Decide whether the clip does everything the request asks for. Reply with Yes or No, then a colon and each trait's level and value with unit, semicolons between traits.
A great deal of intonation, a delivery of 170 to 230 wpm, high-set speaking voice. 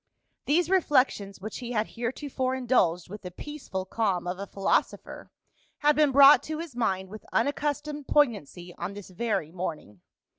No: wide, 7.4 semitones; average, 155 wpm; high, 230 Hz